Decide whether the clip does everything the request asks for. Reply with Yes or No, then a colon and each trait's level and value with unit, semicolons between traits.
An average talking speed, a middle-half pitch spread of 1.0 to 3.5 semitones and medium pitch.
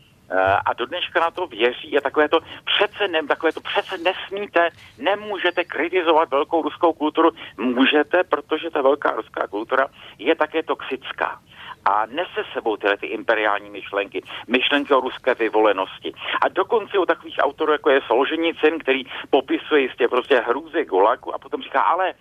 No: average, 155 wpm; average, 4.3 semitones; medium, 160 Hz